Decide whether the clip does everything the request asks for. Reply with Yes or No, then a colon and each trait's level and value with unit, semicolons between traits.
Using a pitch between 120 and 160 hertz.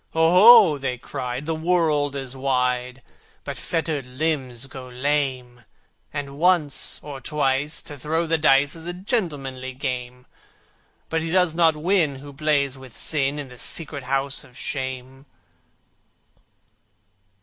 Yes: medium, 140 Hz